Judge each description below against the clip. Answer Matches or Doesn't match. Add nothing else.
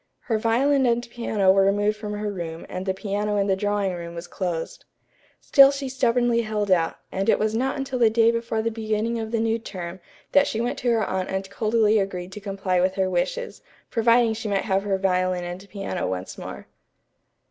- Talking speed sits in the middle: Doesn't match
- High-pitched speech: Matches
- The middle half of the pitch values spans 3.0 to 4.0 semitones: Matches